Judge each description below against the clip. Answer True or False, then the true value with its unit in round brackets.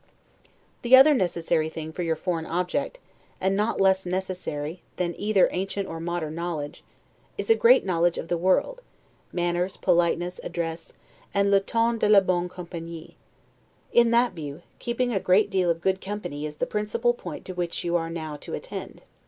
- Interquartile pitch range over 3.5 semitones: False (3.2 semitones)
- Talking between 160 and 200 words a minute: True (175 wpm)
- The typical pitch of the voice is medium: True (180 Hz)